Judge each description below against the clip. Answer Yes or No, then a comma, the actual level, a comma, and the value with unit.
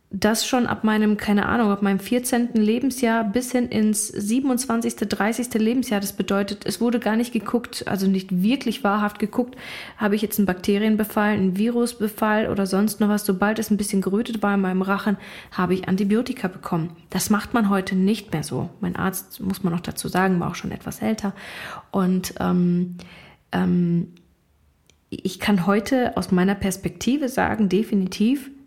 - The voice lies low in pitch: No, high, 205 Hz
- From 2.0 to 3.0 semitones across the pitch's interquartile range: Yes, average, 2.7 semitones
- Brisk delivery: No, average, 170 wpm